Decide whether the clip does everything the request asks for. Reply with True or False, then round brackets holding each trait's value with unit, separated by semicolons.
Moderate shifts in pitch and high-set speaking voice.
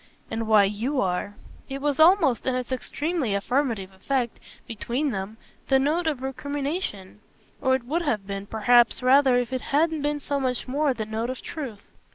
True (4.6 semitones; 255 Hz)